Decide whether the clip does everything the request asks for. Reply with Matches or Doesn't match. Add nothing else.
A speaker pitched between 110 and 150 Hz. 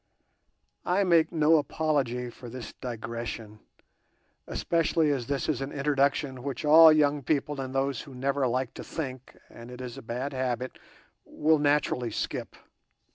Matches